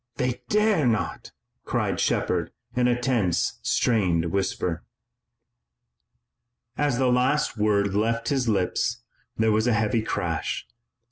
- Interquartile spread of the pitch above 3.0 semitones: Yes, average, 3.6 semitones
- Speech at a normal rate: No, slow, 120 wpm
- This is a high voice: No, low, 115 Hz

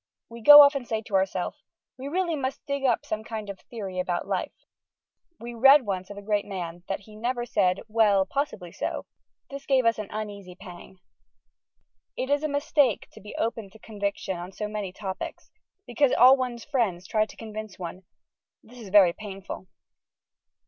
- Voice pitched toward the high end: Yes, high, 215 Hz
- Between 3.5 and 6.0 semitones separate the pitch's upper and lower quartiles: Yes, average, 4.5 semitones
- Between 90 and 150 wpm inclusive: No, average, 185 wpm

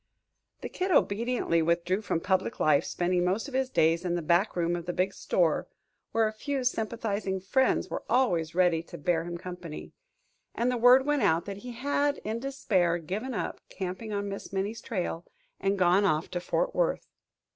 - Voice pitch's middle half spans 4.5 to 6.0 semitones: Yes, wide, 5.4 semitones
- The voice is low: No, high, 195 Hz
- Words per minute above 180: Yes, average, 190 wpm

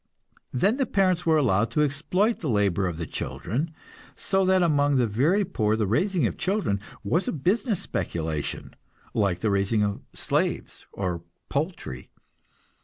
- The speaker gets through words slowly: No, average, 155 wpm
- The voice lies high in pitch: No, low, 135 Hz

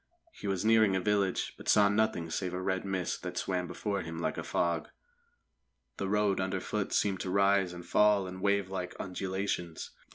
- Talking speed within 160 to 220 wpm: Yes, average, 175 wpm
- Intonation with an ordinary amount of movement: No, narrow, 1.8 semitones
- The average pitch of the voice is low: Yes, very low, 95 Hz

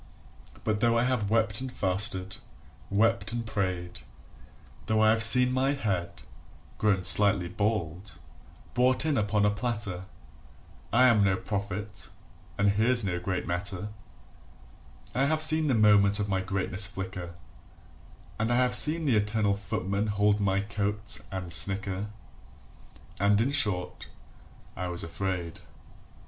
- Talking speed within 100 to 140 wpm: Yes, slow, 135 wpm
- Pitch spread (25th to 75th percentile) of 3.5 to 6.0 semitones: No, average, 3.0 semitones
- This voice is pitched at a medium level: No, low, 105 Hz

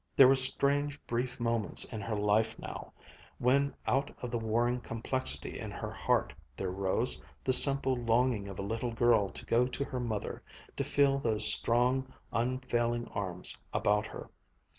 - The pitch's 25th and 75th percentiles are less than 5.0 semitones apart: Yes, average, 2.8 semitones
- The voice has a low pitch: Yes, low, 120 Hz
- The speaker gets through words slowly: No, average, 160 wpm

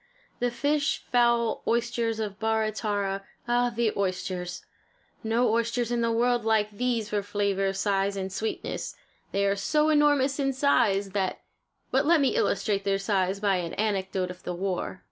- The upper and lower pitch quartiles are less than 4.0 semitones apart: Yes, average, 3.5 semitones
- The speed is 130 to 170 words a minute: Yes, average, 165 wpm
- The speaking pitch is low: No, high, 215 Hz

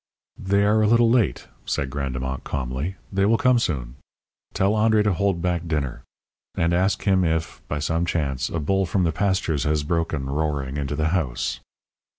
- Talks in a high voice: No, very low, 80 Hz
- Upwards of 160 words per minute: Yes, average, 175 wpm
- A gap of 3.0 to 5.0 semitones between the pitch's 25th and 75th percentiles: No, wide, 5.6 semitones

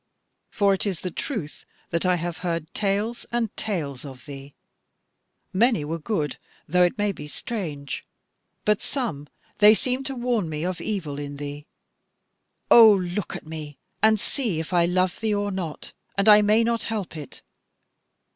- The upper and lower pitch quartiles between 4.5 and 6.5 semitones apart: Yes, wide, 5.6 semitones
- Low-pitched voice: No, medium, 185 Hz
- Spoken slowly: No, average, 165 wpm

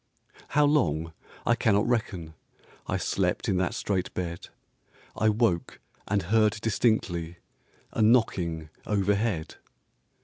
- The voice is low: Yes, low, 100 Hz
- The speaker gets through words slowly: Yes, slow, 110 wpm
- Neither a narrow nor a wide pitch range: Yes, average, 4.6 semitones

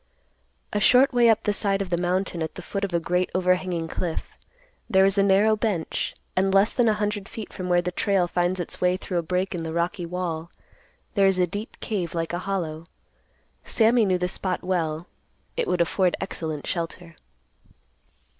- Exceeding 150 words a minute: Yes, average, 190 wpm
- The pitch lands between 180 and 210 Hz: Yes, medium, 185 Hz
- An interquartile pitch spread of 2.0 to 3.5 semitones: Yes, narrow, 2.4 semitones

